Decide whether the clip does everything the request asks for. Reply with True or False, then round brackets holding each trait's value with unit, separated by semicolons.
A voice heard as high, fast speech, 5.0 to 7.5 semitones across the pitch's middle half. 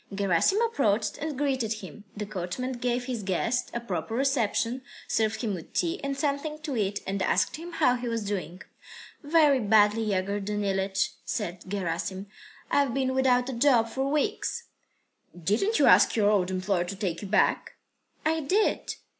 False (225 Hz; 165 wpm; 5.3 semitones)